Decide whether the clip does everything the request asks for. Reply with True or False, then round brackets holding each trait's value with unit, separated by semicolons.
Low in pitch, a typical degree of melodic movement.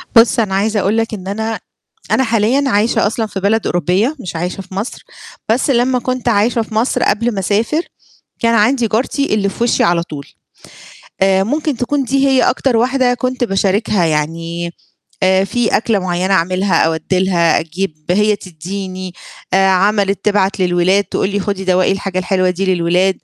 False (200 Hz; 3.6 semitones)